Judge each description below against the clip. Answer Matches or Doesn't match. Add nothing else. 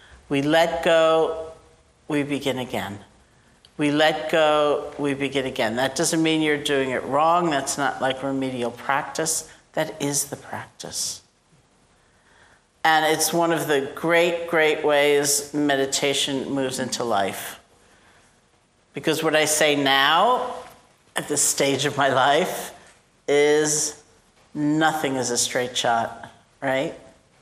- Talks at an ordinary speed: Doesn't match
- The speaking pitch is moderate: Matches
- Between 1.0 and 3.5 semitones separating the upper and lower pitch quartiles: Matches